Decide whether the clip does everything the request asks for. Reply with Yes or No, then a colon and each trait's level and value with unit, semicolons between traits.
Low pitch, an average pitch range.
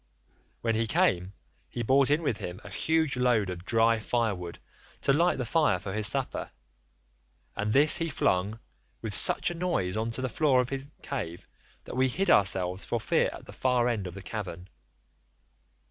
No: low, 115 Hz; wide, 5.8 semitones